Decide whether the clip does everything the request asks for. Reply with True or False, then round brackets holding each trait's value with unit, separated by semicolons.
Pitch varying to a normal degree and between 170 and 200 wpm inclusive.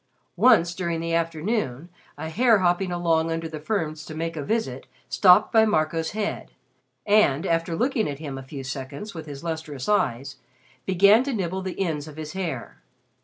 True (4.0 semitones; 175 wpm)